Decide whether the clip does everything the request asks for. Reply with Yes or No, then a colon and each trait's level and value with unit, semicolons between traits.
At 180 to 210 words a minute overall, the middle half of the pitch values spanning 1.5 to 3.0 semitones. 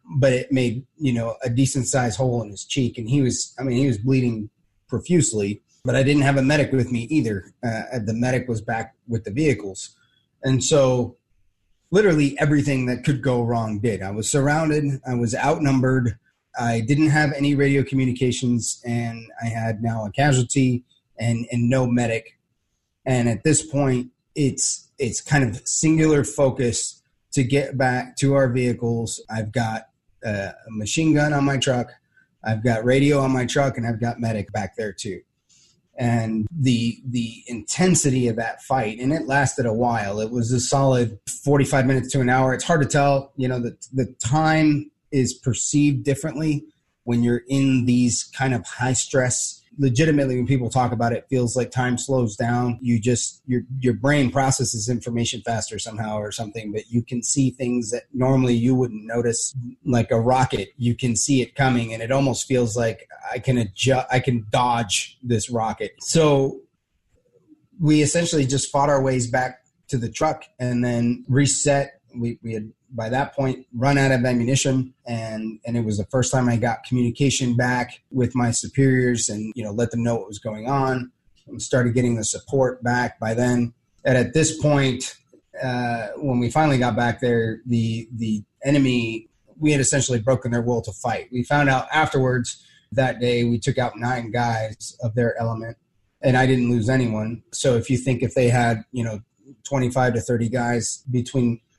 Yes: average, 185 wpm; narrow, 2.5 semitones